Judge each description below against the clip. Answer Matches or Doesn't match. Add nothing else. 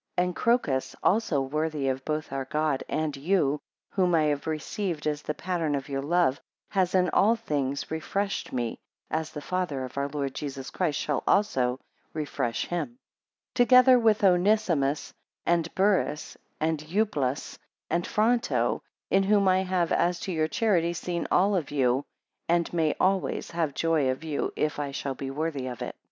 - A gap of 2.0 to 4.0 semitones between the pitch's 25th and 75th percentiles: Doesn't match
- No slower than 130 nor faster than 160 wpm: Doesn't match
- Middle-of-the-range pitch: Matches